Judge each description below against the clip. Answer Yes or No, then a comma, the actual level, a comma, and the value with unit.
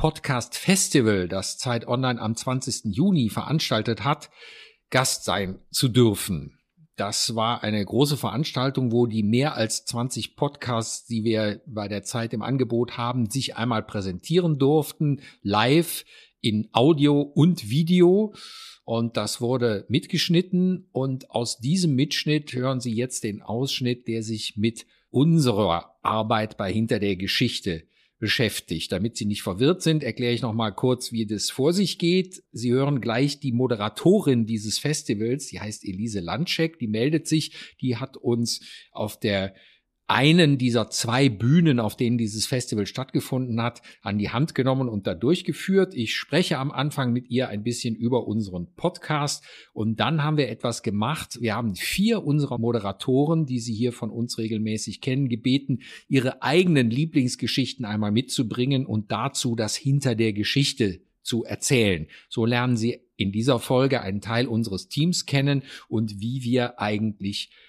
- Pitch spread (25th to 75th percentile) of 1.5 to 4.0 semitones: No, average, 4.4 semitones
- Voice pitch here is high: No, low, 125 Hz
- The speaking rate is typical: Yes, average, 155 wpm